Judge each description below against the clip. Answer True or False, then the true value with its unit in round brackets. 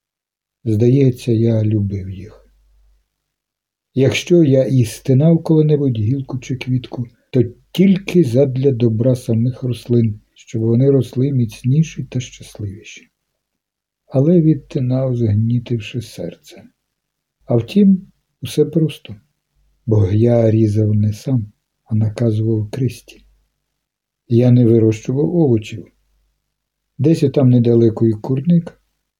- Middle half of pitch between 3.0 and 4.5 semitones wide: True (3.6 semitones)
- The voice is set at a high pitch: False (125 Hz)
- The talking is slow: True (100 wpm)